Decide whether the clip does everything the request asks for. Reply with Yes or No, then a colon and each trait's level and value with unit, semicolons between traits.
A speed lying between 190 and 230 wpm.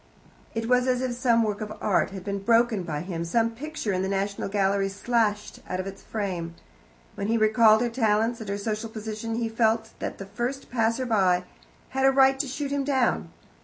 Yes: average, 200 wpm